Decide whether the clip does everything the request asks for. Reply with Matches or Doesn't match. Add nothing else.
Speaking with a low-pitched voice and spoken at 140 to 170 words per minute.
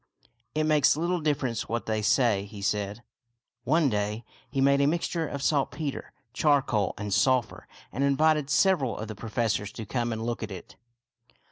Doesn't match